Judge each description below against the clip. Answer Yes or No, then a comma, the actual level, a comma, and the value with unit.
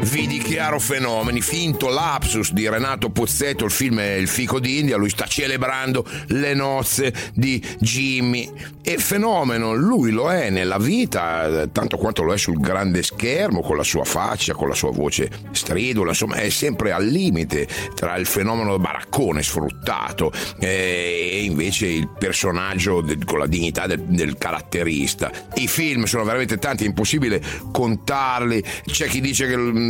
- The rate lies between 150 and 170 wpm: Yes, average, 155 wpm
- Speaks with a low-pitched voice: Yes, low, 115 Hz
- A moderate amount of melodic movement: No, wide, 5.7 semitones